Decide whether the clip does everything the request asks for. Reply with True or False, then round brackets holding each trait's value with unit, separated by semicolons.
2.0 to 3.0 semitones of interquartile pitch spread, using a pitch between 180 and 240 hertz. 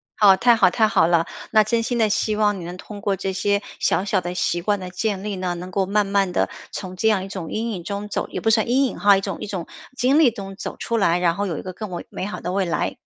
True (2.7 semitones; 200 Hz)